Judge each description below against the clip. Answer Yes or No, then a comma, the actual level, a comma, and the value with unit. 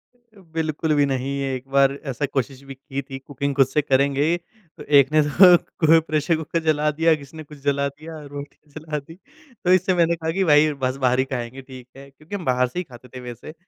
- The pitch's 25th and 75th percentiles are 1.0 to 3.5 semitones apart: Yes, average, 2.7 semitones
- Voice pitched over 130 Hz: Yes, medium, 140 Hz